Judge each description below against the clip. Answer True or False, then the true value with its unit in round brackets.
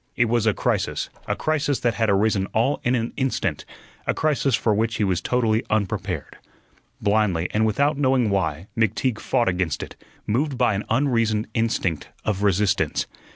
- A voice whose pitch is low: True (110 Hz)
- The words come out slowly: False (165 wpm)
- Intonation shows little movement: False (3.4 semitones)